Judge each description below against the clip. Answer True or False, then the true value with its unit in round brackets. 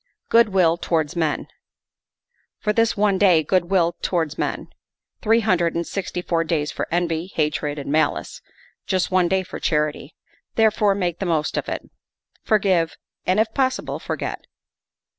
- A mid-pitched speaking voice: True (175 Hz)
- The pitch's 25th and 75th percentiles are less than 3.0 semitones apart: False (3.7 semitones)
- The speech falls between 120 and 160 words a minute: True (155 wpm)